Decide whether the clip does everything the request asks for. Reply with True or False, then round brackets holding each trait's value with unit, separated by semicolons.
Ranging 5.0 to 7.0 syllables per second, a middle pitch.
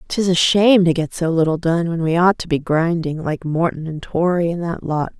True (5.2 syllables/s; 170 Hz)